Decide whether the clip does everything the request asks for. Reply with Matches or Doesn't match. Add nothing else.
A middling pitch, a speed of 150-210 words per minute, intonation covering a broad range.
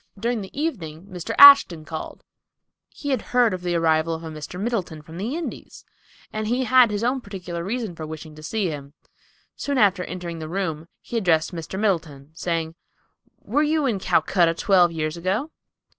Matches